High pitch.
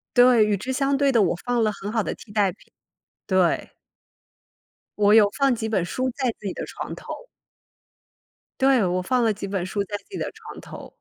Yes: high, 215 Hz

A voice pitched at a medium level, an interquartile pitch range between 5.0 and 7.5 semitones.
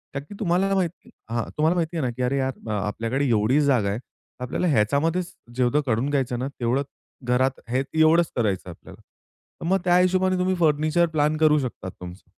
Yes: medium, 145 Hz; wide, 5.6 semitones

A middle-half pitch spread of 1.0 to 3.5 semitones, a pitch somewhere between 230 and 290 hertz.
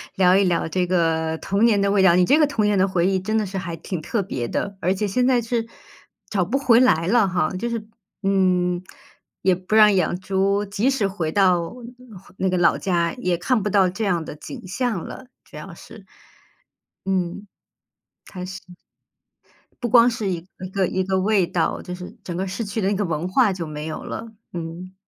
No: average, 2.9 semitones; high, 190 Hz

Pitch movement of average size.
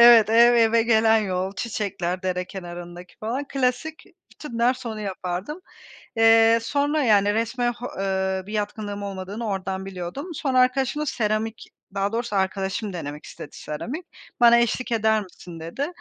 Yes: average, 3.9 semitones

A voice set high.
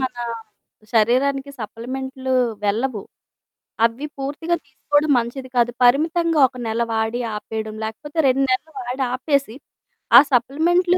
Yes: very high, 260 Hz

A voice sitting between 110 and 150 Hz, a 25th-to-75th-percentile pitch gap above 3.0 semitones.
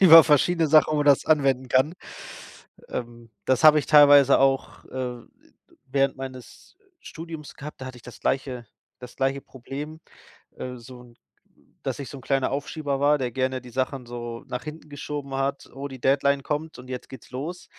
No: low, 135 Hz; narrow, 2.4 semitones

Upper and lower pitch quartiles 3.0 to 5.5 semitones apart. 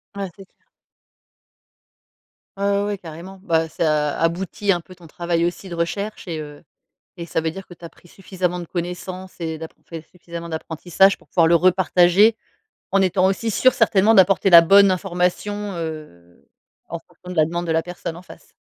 No: narrow, 2.6 semitones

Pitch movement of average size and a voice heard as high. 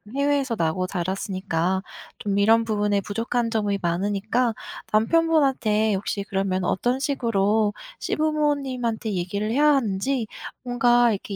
Yes: average, 4.2 semitones; high, 220 Hz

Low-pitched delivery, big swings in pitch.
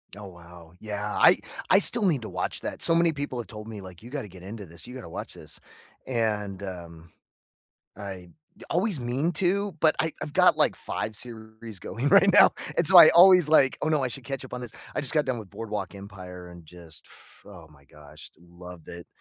Yes: low, 110 Hz; wide, 8.0 semitones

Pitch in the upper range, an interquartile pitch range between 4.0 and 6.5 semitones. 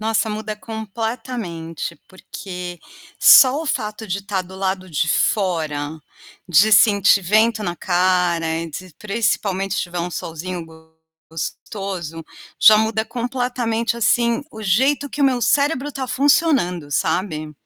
Yes: high, 205 Hz; average, 4.6 semitones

